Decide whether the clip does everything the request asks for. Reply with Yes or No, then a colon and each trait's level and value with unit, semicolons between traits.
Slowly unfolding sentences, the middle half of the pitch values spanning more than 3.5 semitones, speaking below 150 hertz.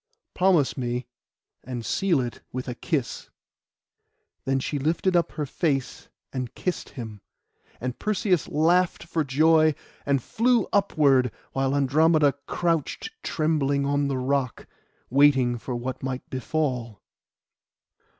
Yes: slow, 120 wpm; average, 3.9 semitones; medium, 140 Hz